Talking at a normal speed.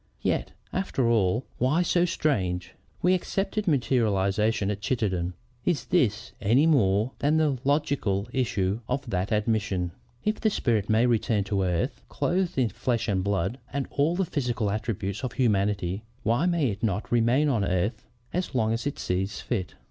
Yes: average, 165 wpm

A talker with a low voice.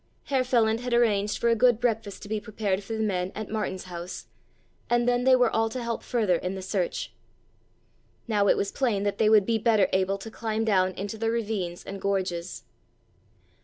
No: high, 215 Hz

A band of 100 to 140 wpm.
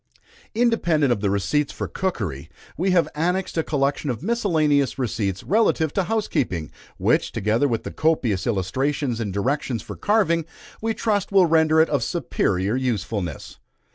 No: average, 150 wpm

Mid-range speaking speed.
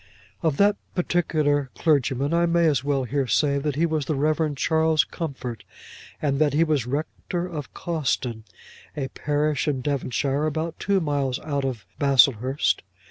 Yes: average, 155 wpm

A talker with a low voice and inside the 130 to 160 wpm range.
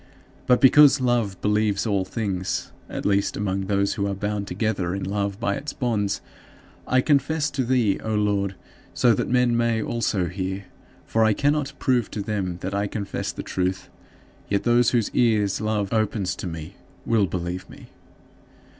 No: low, 105 Hz; average, 170 wpm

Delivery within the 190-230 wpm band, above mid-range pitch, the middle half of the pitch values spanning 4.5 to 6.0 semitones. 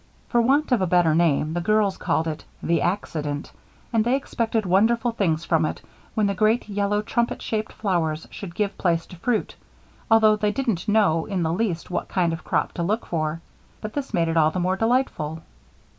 Yes: average, 200 wpm; high, 195 Hz; average, 4.8 semitones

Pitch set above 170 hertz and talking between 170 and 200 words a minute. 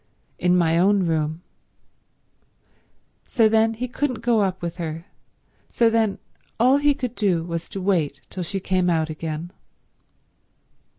No: medium, 185 Hz; average, 140 wpm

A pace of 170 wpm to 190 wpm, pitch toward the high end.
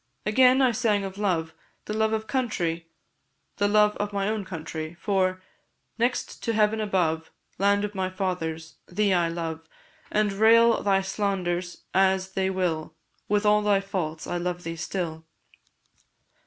No: average, 155 wpm; high, 195 Hz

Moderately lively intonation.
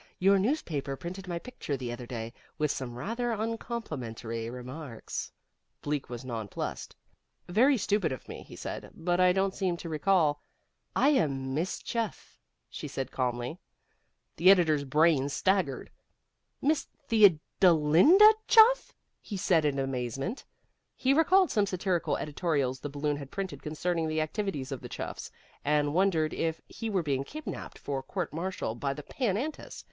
No: wide, 6.4 semitones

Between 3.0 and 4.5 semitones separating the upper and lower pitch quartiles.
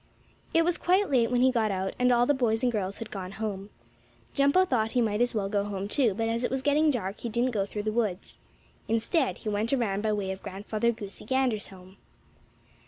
Yes: average, 3.7 semitones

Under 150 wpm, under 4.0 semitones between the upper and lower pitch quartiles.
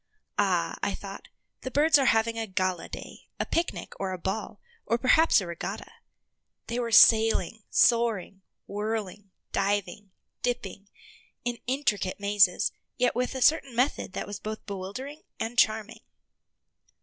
Yes: average, 140 wpm; average, 3.6 semitones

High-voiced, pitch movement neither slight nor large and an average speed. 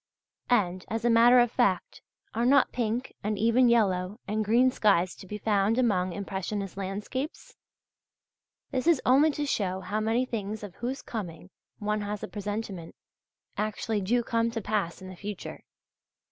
Yes: high, 215 Hz; average, 3.5 semitones; average, 160 wpm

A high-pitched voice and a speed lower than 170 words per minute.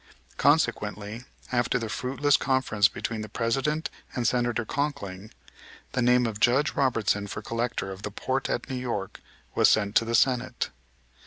No: low, 120 Hz; average, 155 wpm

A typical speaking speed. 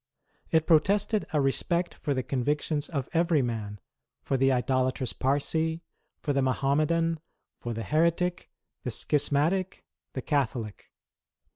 No: slow, 125 wpm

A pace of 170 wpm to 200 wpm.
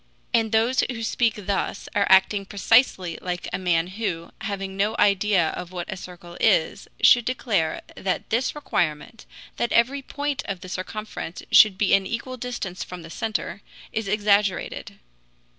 No: average, 160 wpm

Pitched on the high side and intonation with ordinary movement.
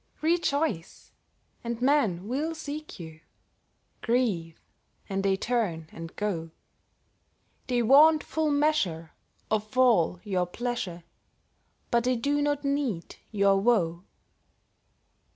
No: high, 230 Hz; wide, 8.0 semitones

